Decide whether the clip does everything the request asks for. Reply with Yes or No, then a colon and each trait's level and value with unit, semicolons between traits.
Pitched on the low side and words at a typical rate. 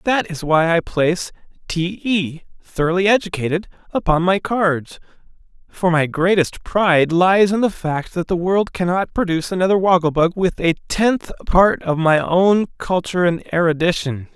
No: medium, 180 Hz; average, 160 wpm